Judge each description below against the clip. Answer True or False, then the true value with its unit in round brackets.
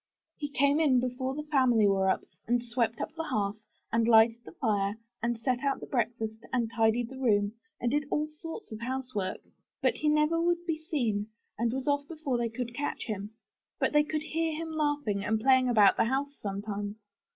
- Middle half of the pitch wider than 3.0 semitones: True (4.8 semitones)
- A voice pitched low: False (245 Hz)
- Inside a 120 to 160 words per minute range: False (205 wpm)